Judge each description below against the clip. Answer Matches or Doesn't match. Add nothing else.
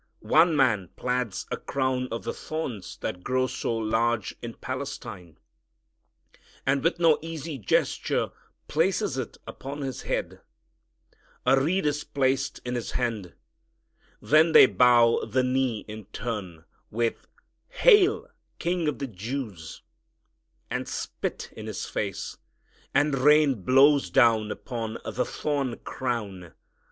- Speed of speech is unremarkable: Doesn't match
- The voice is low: Matches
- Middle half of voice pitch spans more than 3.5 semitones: Matches